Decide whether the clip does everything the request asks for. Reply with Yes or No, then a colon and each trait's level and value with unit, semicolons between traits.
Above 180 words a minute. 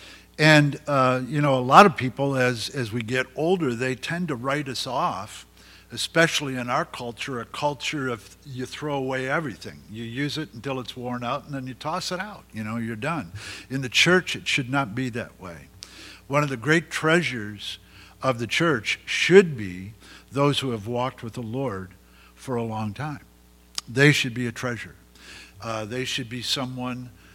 Yes: average, 190 wpm